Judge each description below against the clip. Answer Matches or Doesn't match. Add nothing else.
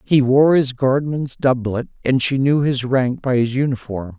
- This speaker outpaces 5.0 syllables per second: Doesn't match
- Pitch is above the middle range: Doesn't match